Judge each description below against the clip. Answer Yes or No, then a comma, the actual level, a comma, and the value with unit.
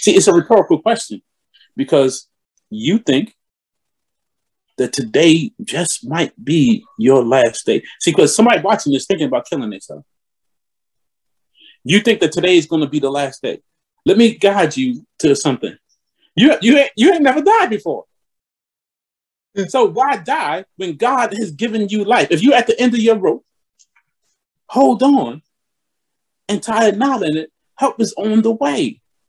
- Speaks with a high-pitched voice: Yes, high, 225 Hz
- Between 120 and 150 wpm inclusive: No, average, 165 wpm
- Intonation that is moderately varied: No, wide, 6.0 semitones